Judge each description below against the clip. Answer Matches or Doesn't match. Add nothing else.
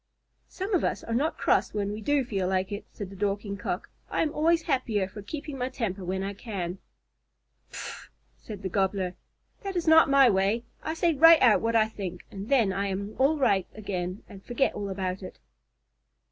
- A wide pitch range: Matches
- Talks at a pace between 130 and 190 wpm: Doesn't match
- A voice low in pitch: Doesn't match